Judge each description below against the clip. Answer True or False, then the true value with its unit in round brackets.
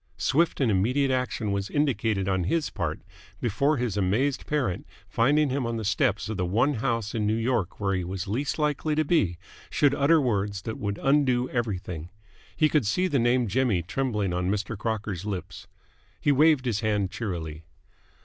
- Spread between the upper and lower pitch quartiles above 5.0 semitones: True (5.6 semitones)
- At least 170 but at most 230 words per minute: True (180 wpm)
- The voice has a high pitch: False (115 Hz)